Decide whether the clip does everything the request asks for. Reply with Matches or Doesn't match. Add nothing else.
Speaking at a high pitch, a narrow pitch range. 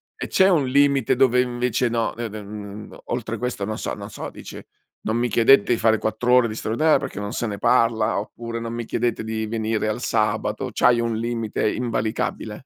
Doesn't match